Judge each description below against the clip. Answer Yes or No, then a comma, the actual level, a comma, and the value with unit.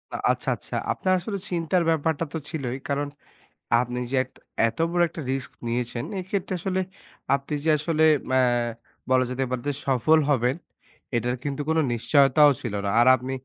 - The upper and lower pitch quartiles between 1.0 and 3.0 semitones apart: No, average, 4.3 semitones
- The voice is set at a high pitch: No, medium, 140 Hz